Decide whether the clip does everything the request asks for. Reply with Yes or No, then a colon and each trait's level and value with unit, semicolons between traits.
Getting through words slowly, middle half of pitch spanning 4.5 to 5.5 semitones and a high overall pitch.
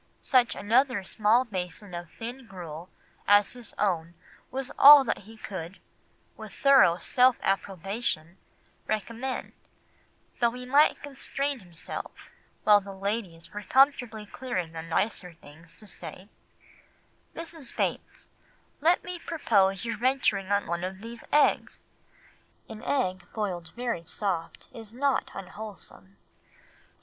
Yes: slow, 125 wpm; average, 5.2 semitones; high, 210 Hz